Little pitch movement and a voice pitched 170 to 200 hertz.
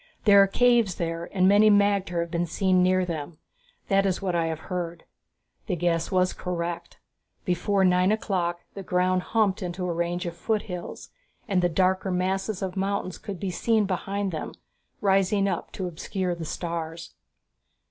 Yes: narrow, 2.2 semitones; medium, 185 Hz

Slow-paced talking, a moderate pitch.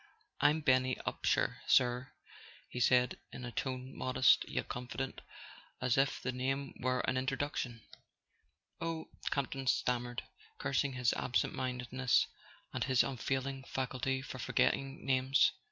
No: slow, 130 wpm; low, 130 Hz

